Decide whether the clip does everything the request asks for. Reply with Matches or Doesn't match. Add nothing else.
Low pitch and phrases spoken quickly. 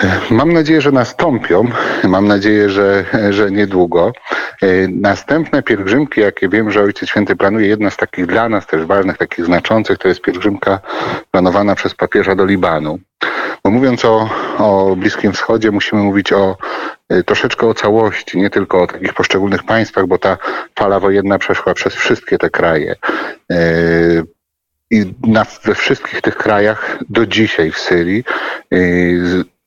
Doesn't match